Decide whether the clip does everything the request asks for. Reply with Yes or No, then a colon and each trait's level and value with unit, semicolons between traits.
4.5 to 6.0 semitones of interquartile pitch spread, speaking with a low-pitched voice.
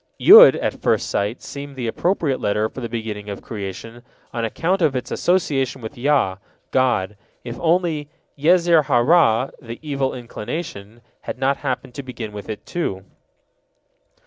Yes: average, 5.0 semitones; low, 125 Hz